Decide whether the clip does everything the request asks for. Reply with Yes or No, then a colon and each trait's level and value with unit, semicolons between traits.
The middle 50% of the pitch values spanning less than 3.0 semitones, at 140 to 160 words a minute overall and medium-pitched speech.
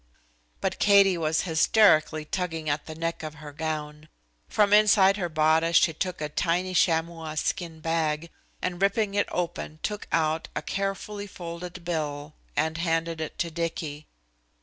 Yes: narrow, 2.6 semitones; average, 150 wpm; medium, 165 Hz